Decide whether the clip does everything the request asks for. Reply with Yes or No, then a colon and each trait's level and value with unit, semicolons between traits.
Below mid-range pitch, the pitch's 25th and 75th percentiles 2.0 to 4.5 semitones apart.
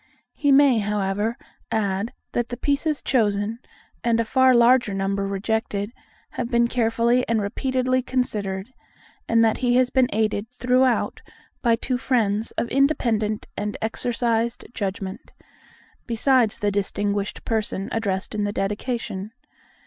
No: high, 225 Hz; average, 3.4 semitones